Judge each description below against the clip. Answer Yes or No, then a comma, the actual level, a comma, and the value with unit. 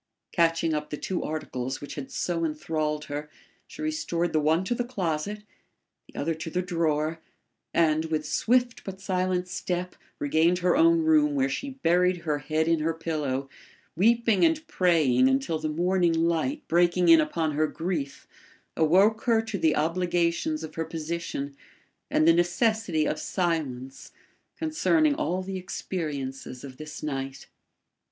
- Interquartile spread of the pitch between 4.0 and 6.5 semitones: No, average, 3.5 semitones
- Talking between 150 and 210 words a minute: Yes, average, 155 wpm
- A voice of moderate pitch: Yes, medium, 165 Hz